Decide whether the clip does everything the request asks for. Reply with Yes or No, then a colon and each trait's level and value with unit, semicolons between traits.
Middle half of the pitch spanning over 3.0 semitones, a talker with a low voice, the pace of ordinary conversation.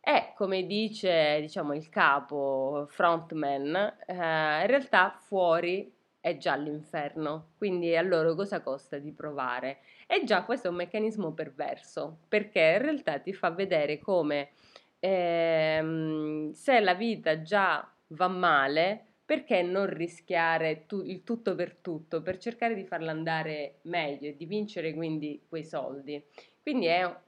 No: average, 4.0 semitones; medium, 170 Hz; average, 140 wpm